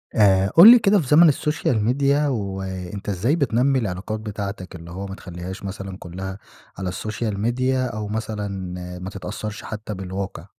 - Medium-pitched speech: No, low, 105 Hz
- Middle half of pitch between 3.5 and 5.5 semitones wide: Yes, average, 4.5 semitones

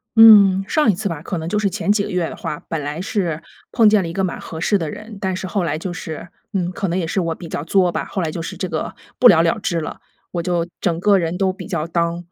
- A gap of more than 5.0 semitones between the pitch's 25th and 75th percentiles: No, average, 3.1 semitones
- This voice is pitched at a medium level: Yes, medium, 180 Hz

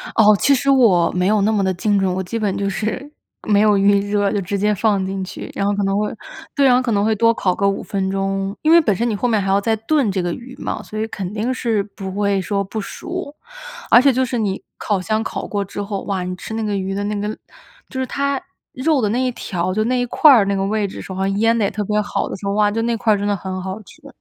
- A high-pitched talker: Yes, high, 205 Hz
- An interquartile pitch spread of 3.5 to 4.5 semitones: No, average, 2.8 semitones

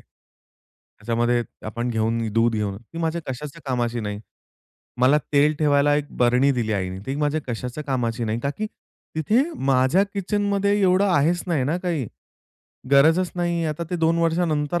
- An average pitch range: No, wide, 5.9 semitones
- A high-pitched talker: No, medium, 145 Hz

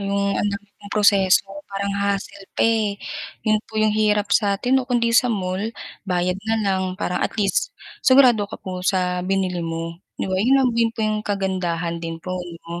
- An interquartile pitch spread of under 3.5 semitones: Yes, average, 2.8 semitones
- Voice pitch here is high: Yes, high, 200 Hz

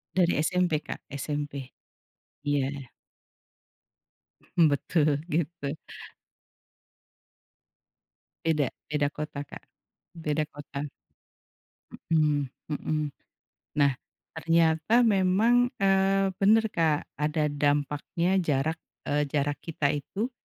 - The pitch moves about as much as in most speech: Yes, average, 3.3 semitones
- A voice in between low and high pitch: Yes, medium, 155 Hz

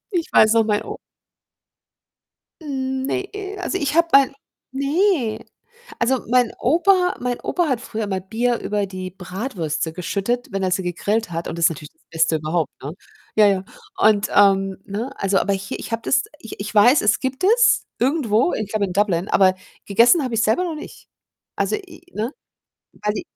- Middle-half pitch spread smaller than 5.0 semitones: No, wide, 5.6 semitones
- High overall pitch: Yes, high, 220 Hz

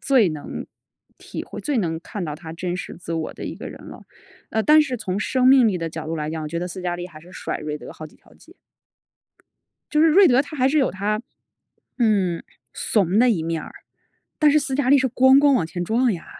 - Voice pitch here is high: Yes, high, 200 Hz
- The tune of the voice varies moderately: No, wide, 7.8 semitones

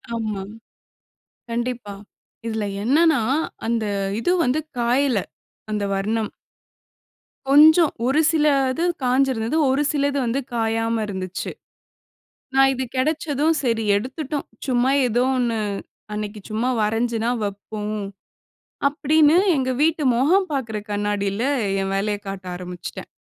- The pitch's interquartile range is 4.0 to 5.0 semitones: Yes, average, 4.7 semitones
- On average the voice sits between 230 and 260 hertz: Yes, high, 235 Hz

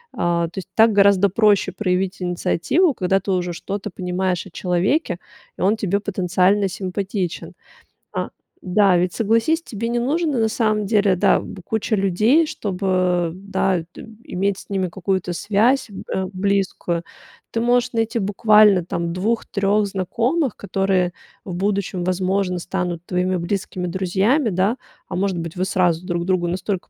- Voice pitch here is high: Yes, high, 195 Hz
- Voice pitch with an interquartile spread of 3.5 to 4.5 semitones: No, average, 2.7 semitones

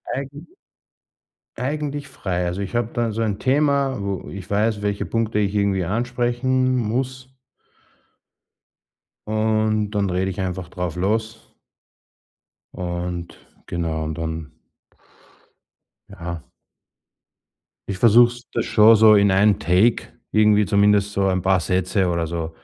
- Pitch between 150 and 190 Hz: No, low, 105 Hz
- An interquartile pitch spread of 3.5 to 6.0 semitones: Yes, average, 4.2 semitones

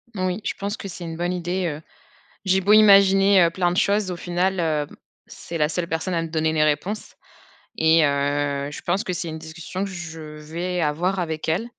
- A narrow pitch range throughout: No, average, 3.0 semitones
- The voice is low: No, medium, 175 Hz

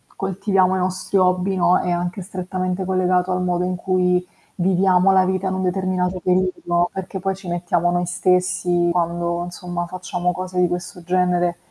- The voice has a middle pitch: Yes, medium, 180 Hz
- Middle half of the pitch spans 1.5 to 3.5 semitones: No, narrow, 0.9 semitones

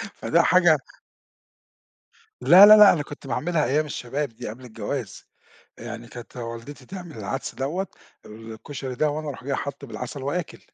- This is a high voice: No, medium, 140 Hz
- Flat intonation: No, average, 4.6 semitones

